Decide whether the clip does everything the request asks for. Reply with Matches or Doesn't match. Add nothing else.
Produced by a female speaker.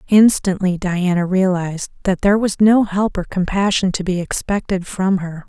Matches